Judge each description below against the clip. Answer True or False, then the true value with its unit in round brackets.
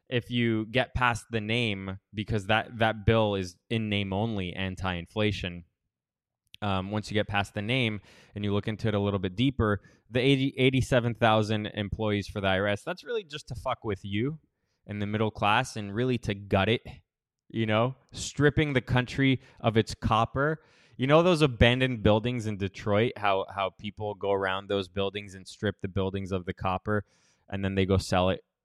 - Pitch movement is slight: False (3.5 semitones)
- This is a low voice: True (105 Hz)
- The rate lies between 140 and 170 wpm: False (185 wpm)